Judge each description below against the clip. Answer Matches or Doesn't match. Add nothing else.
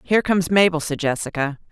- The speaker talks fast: Doesn't match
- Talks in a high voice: Doesn't match